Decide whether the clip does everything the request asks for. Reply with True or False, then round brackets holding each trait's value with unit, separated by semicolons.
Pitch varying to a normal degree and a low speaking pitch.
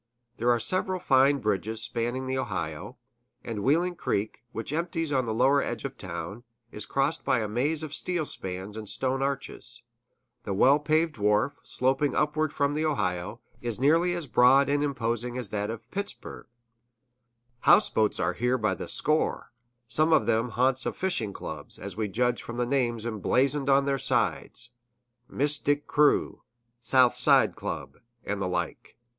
True (4.3 semitones; 125 Hz)